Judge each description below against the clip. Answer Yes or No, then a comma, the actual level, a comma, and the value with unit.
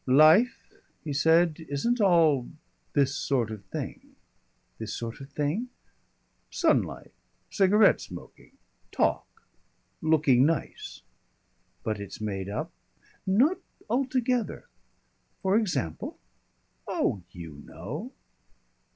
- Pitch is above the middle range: No, medium, 150 Hz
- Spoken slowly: Yes, slow, 100 wpm